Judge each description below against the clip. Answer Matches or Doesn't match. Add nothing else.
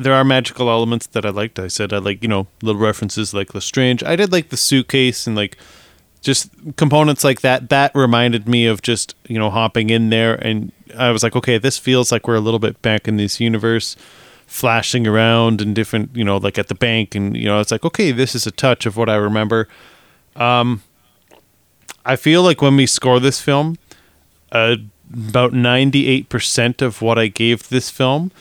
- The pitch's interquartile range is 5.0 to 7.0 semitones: Doesn't match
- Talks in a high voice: Doesn't match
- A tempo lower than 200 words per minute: Doesn't match